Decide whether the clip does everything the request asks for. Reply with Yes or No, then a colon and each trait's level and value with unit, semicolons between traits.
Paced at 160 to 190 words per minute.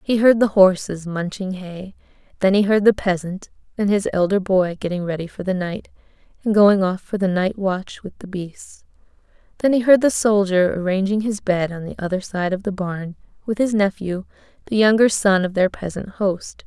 No: average, 200 wpm